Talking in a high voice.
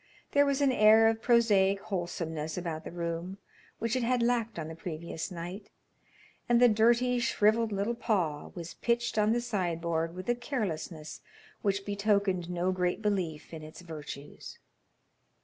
Yes: high, 195 Hz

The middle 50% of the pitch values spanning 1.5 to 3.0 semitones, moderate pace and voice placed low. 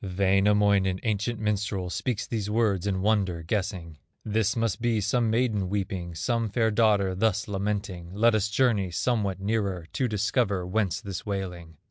Yes: narrow, 2.6 semitones; average, 150 wpm; low, 100 Hz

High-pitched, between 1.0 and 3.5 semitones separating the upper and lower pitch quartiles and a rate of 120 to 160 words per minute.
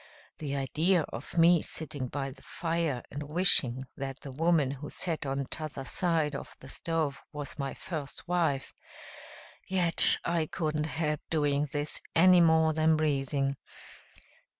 No: medium, 150 Hz; average, 3.0 semitones; average, 150 wpm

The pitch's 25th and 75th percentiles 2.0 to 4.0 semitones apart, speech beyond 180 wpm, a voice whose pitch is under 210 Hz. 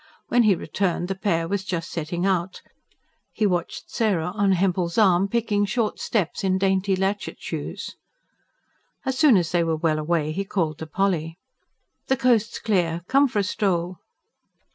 No: average, 3.2 semitones; average, 165 wpm; high, 190 Hz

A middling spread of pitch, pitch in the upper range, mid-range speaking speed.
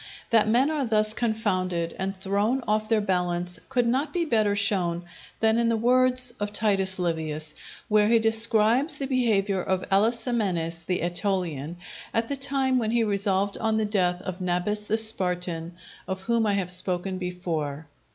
Yes: average, 4.0 semitones; high, 205 Hz; average, 165 wpm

